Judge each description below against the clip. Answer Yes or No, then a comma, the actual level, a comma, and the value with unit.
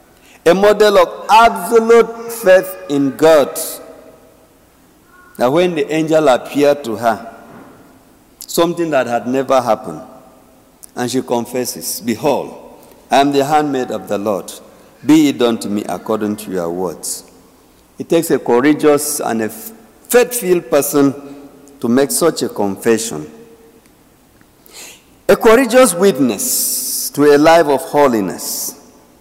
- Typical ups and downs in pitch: No, wide, 6.2 semitones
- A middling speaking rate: No, slow, 125 wpm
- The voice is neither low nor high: Yes, medium, 145 Hz